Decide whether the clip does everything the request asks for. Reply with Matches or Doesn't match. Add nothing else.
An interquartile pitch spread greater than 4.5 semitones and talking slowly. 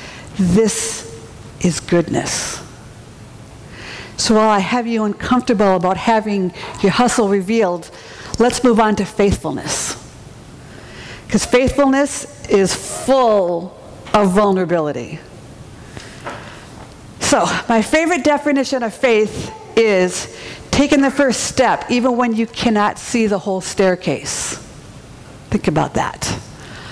Matches